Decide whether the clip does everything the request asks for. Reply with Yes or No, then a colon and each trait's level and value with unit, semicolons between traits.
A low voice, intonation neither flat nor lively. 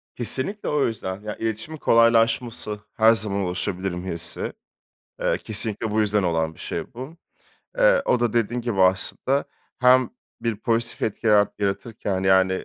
Yes: low, 110 Hz; average, 3.6 semitones